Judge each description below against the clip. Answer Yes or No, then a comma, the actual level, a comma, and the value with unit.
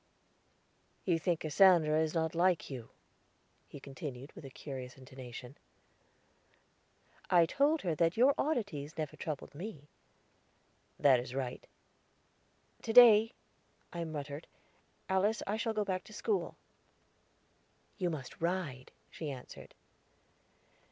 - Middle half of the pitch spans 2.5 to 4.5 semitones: No, wide, 5.4 semitones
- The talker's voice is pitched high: No, medium, 160 Hz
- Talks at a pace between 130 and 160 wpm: No, slow, 120 wpm